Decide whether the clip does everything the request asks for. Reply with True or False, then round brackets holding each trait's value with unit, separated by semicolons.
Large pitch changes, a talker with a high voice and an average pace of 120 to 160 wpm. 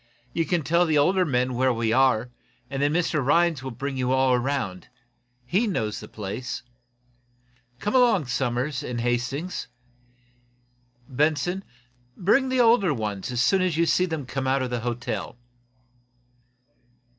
False (5.7 semitones; 135 Hz; 150 wpm)